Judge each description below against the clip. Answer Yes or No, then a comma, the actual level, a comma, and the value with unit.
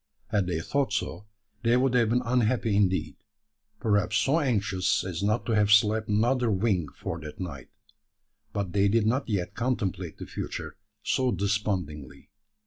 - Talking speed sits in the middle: Yes, average, 155 wpm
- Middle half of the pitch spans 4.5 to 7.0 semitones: No, average, 3.8 semitones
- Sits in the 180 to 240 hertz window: No, low, 105 Hz